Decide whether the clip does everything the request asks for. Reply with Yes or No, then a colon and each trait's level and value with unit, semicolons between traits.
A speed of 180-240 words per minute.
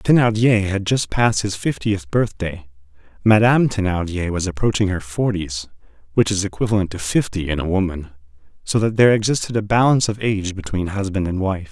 No: average, 170 wpm